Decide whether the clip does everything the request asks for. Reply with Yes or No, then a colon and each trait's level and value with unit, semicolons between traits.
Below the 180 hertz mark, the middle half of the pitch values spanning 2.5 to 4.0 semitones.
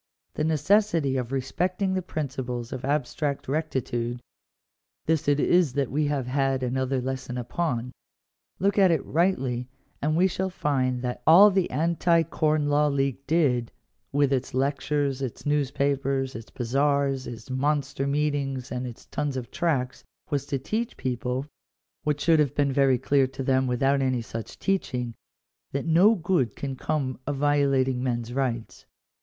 Yes: medium, 140 Hz; average, 2.9 semitones